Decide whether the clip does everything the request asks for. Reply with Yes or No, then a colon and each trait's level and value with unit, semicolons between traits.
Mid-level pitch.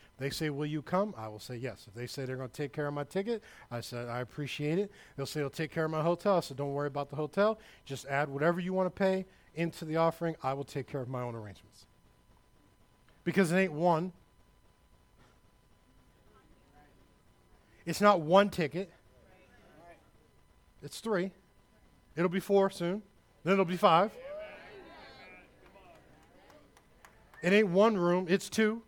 Yes: medium, 165 Hz